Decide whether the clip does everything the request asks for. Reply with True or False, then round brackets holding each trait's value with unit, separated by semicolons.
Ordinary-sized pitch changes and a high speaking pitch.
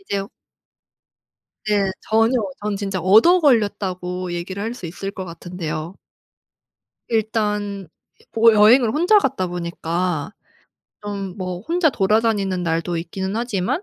True (3.7 semitones; 200 Hz)